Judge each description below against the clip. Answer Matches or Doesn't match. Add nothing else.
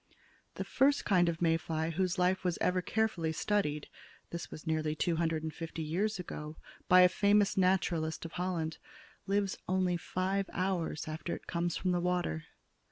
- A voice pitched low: Doesn't match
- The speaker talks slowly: Doesn't match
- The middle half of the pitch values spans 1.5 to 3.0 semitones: Matches